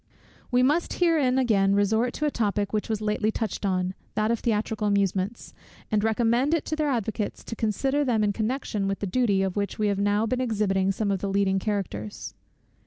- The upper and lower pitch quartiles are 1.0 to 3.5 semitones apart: Yes, average, 3.2 semitones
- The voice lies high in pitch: Yes, high, 215 Hz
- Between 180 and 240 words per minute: Yes, average, 200 wpm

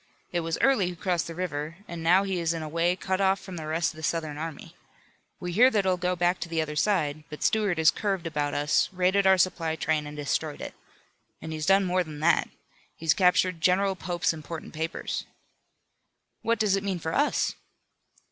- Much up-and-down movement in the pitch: No, average, 3.0 semitones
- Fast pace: Yes, fast, 210 wpm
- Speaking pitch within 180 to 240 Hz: No, medium, 170 Hz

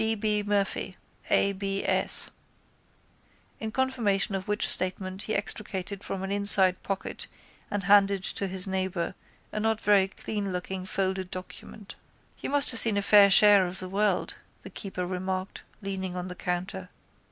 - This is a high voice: Yes, high, 195 Hz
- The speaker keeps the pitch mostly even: Yes, narrow, 1.7 semitones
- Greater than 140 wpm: Yes, average, 155 wpm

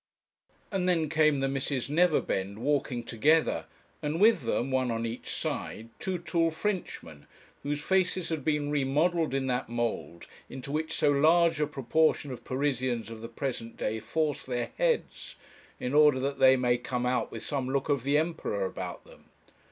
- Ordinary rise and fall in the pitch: Yes, average, 4.2 semitones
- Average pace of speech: Yes, average, 170 wpm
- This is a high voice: No, medium, 140 Hz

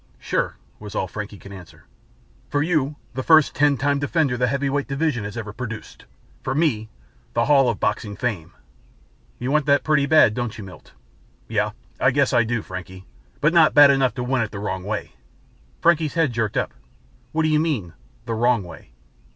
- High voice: No, low, 125 Hz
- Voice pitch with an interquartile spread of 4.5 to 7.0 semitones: Yes, average, 5.2 semitones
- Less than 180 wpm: No, average, 190 wpm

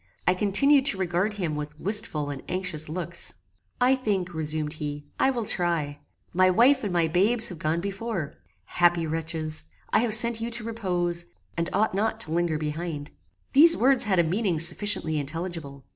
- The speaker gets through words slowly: No, average, 175 wpm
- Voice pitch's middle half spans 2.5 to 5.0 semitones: No, wide, 5.4 semitones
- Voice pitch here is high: No, medium, 175 Hz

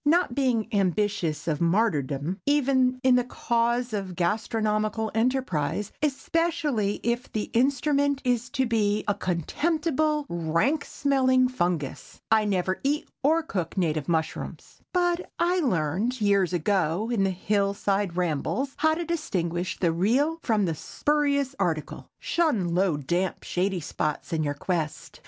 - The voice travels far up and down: Yes, wide, 7.3 semitones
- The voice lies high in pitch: Yes, high, 215 Hz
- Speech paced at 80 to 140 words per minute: Yes, slow, 135 wpm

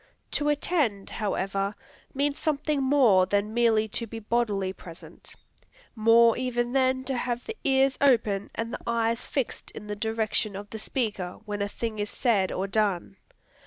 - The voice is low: No, high, 225 Hz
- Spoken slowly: No, average, 160 wpm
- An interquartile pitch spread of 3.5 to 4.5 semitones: Yes, average, 4.0 semitones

